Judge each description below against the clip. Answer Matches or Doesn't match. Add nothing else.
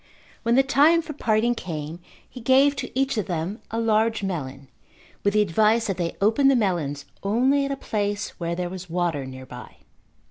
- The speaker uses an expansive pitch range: Matches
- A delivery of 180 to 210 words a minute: Matches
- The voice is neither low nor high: Doesn't match